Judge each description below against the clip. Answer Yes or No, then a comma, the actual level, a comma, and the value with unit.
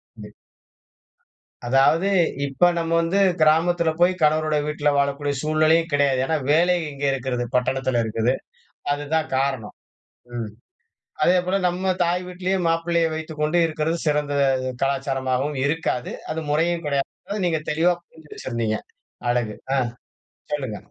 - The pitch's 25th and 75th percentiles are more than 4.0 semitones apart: No, average, 3.5 semitones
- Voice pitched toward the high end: No, medium, 150 Hz